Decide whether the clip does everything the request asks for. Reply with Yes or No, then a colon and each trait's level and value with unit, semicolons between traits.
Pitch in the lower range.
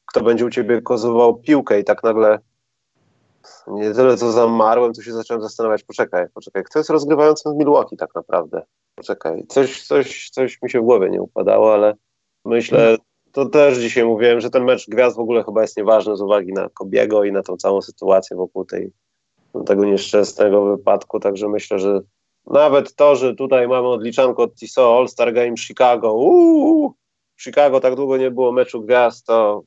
Yes: low, 120 Hz